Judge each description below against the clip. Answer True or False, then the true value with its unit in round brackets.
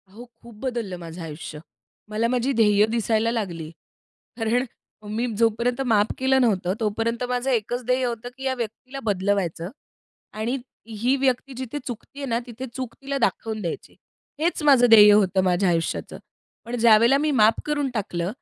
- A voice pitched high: True (230 Hz)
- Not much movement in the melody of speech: False (3.4 semitones)